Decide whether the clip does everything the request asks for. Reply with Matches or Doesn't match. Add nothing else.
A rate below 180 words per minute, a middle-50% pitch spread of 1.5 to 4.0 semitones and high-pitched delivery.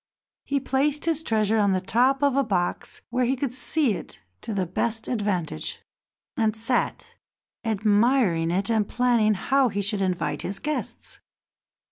Doesn't match